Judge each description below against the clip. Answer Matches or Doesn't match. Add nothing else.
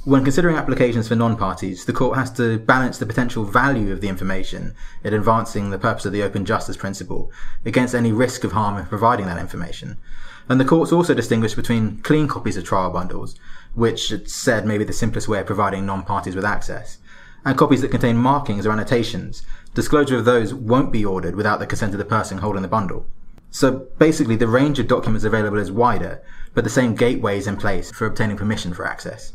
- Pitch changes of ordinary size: Matches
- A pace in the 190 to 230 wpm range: Matches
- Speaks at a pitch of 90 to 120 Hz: Matches